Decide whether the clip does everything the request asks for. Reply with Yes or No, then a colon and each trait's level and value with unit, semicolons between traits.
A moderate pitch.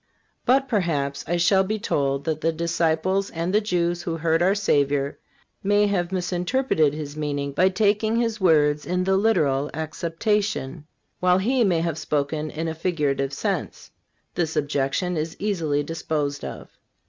Yes: medium, 165 Hz